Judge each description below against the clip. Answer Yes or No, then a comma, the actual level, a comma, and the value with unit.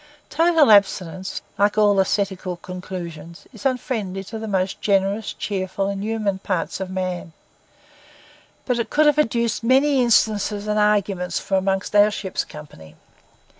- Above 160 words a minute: No, average, 140 wpm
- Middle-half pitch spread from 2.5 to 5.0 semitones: Yes, average, 2.8 semitones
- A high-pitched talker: Yes, high, 200 Hz